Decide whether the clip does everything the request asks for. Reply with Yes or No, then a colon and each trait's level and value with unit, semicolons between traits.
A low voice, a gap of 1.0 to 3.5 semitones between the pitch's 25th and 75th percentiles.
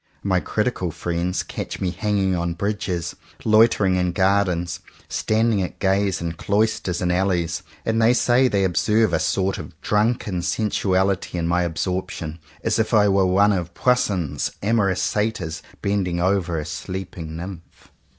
Yes: very low, 95 Hz; average, 3.0 semitones